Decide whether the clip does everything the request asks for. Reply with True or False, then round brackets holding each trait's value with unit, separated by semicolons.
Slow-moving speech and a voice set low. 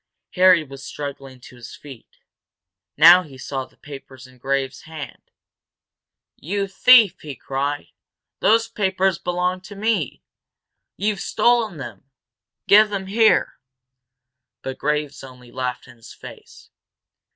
False (125 wpm; 150 Hz)